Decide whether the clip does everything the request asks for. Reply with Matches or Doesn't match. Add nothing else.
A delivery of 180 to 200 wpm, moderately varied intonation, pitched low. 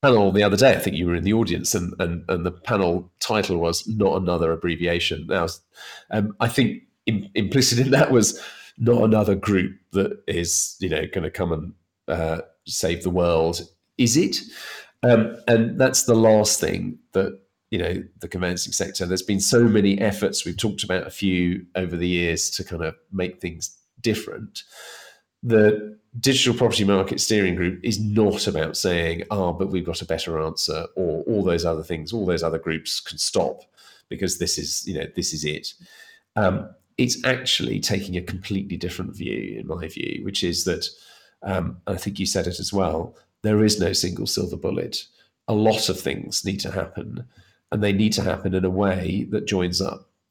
Matches